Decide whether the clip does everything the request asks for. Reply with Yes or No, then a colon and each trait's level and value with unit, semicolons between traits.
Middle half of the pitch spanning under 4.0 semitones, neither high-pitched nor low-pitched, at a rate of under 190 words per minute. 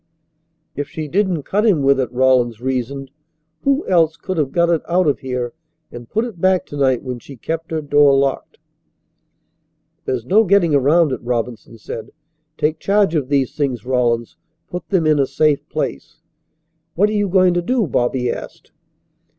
No: wide, 5.4 semitones; medium, 145 Hz; average, 175 wpm